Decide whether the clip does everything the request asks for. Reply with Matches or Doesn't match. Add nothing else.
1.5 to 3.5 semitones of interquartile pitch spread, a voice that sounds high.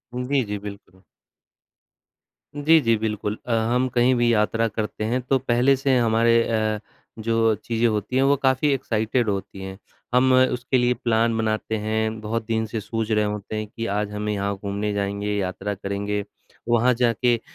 Doesn't match